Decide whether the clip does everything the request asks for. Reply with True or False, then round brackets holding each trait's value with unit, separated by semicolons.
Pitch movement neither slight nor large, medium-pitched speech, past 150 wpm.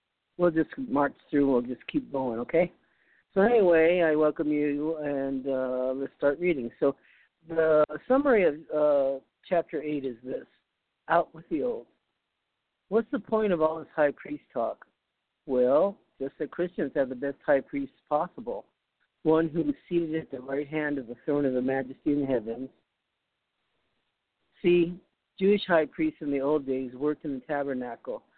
True (4.0 semitones; 150 Hz; 165 wpm)